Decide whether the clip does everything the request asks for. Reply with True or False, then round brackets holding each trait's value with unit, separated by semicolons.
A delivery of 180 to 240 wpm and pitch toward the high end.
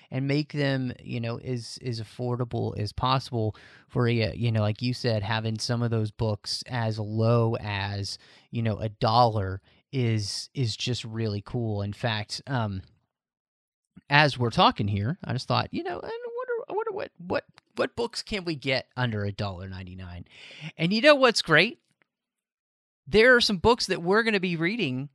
False (185 wpm; 120 Hz)